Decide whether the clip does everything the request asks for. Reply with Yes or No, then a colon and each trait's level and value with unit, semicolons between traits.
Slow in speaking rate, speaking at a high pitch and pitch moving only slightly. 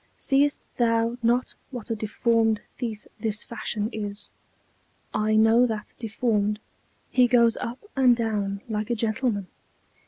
Yes: slow, 130 wpm; high, 225 Hz; narrow, 2.1 semitones